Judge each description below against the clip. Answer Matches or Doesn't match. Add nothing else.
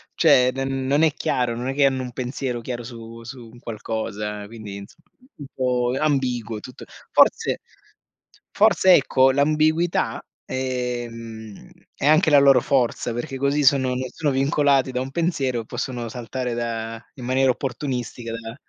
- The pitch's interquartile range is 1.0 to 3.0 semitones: Matches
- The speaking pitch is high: Doesn't match